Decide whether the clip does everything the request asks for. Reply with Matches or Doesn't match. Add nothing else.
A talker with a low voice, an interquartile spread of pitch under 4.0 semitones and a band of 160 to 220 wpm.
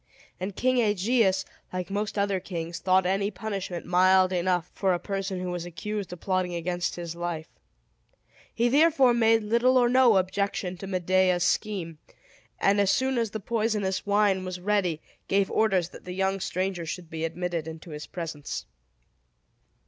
Doesn't match